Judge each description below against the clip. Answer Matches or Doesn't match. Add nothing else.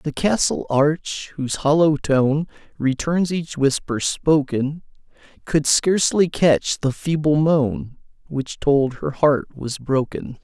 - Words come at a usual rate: Doesn't match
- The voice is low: Doesn't match